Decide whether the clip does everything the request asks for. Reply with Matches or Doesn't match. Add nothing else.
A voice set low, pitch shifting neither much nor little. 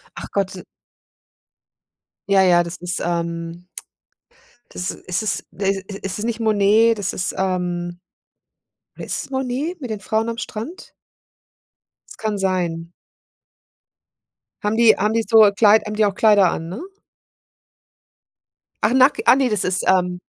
Doesn't match